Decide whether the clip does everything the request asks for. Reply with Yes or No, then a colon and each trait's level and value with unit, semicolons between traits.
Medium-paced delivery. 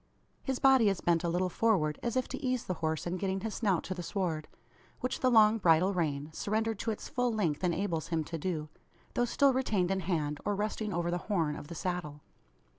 No: fast, 220 wpm